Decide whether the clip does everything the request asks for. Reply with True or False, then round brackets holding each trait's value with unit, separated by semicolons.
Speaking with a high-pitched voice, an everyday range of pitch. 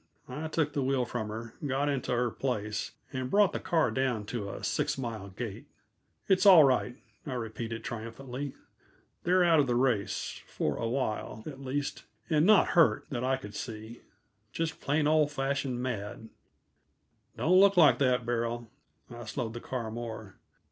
False (125 Hz; 4.0 semitones)